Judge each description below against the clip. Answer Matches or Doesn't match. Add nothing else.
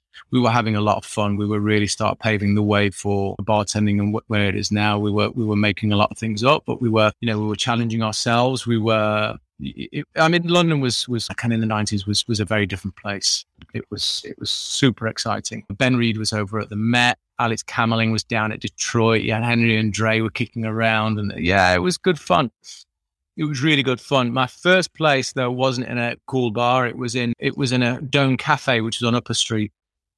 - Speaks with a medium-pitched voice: Doesn't match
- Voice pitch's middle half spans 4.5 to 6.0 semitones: Doesn't match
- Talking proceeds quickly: Matches